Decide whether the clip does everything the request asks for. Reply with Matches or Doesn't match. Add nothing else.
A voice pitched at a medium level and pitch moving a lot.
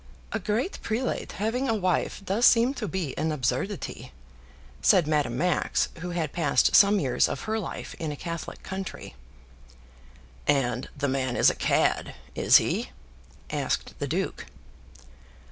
Matches